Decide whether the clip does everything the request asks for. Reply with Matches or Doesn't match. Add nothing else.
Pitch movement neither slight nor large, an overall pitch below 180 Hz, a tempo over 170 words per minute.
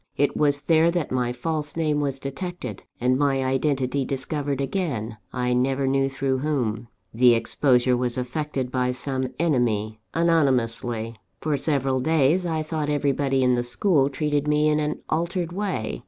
Doesn't match